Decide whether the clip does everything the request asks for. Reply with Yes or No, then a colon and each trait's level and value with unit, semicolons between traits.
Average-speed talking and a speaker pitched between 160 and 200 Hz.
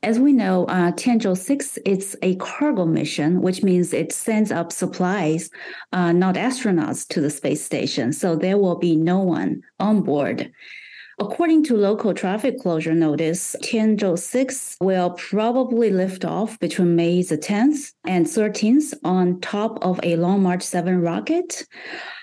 Yes: average, 155 wpm; medium, 185 Hz